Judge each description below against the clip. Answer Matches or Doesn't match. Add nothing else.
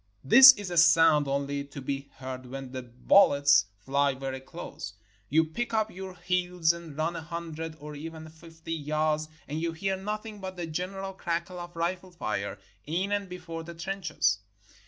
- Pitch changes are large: Doesn't match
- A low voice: Doesn't match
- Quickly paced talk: Doesn't match